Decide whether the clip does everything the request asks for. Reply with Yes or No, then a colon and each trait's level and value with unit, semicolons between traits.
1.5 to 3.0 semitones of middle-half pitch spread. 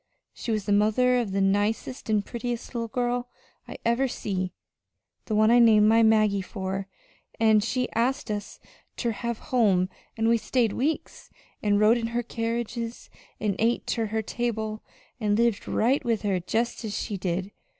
Yes: narrow, 2.4 semitones